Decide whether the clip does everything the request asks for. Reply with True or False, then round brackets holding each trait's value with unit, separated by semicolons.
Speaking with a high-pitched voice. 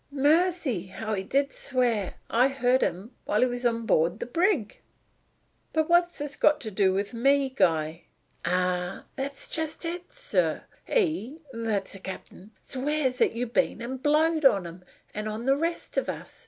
True (250 Hz)